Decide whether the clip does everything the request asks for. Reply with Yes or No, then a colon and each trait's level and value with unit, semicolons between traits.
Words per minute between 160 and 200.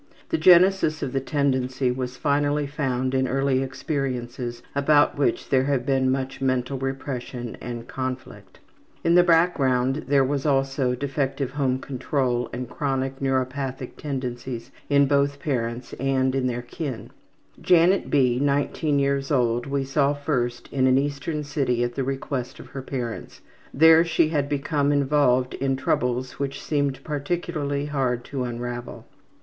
No: average, 145 wpm